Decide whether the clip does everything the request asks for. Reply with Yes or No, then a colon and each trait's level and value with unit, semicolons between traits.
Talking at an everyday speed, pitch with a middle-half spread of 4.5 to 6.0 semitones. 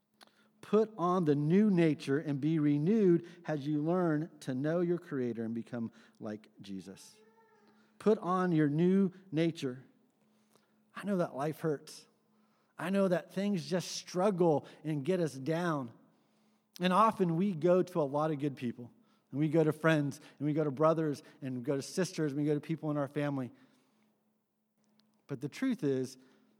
Yes: average, 170 wpm; average, 5.1 semitones